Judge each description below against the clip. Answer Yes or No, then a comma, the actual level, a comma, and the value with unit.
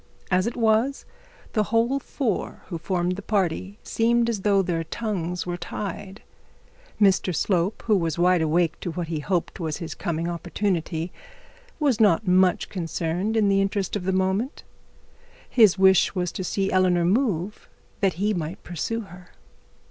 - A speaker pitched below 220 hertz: Yes, high, 190 Hz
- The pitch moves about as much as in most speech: Yes, average, 3.3 semitones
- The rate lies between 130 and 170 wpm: Yes, average, 160 wpm